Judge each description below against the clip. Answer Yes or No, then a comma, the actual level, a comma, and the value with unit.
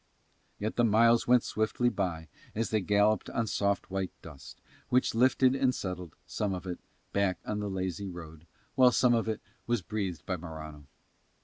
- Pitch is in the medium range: No, low, 100 Hz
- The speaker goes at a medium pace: Yes, average, 175 wpm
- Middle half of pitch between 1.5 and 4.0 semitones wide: No, average, 4.4 semitones